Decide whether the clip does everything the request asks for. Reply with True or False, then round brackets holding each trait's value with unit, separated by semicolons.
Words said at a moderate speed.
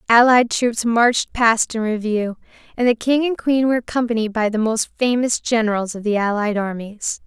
True (180 wpm)